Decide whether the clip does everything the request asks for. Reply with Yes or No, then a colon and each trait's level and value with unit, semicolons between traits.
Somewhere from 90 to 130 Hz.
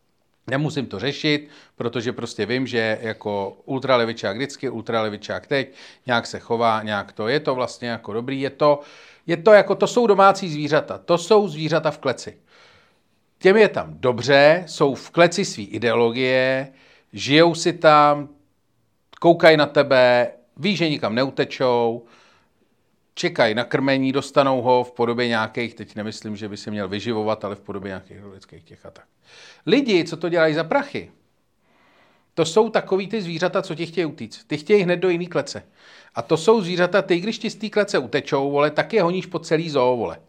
No: medium, 140 Hz